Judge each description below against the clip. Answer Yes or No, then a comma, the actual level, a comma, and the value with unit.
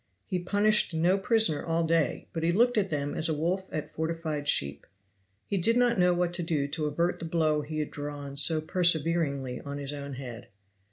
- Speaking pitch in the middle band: Yes, medium, 160 Hz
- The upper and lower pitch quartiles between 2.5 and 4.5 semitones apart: Yes, average, 3.5 semitones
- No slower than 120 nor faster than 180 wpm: No, fast, 205 wpm